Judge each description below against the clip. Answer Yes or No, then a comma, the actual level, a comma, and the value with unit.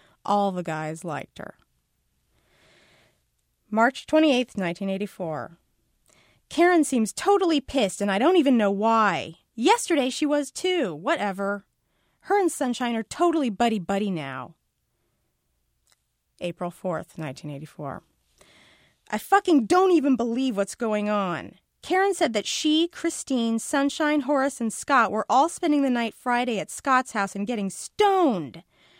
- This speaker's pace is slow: Yes, slow, 130 wpm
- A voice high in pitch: Yes, high, 230 Hz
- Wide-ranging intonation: Yes, wide, 7.4 semitones